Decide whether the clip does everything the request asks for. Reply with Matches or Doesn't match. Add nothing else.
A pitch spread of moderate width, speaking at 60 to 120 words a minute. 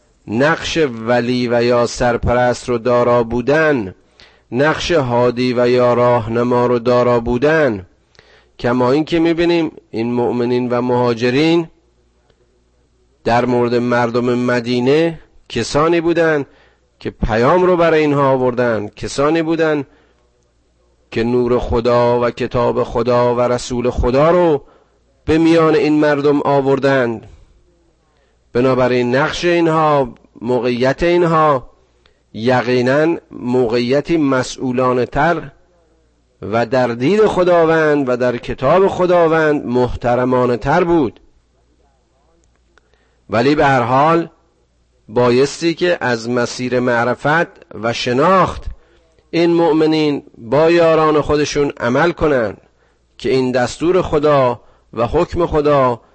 Matches